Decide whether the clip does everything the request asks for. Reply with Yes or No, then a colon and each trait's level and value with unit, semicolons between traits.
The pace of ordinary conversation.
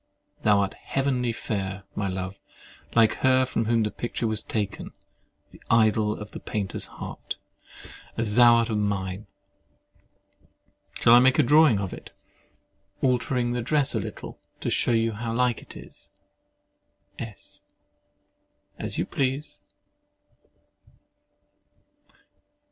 No: slow, 120 wpm